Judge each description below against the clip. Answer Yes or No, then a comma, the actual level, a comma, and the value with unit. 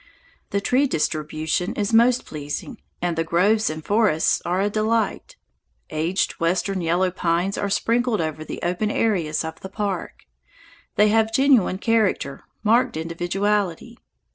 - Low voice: No, high, 195 Hz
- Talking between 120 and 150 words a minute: Yes, average, 140 wpm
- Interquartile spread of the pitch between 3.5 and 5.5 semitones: Yes, average, 4.7 semitones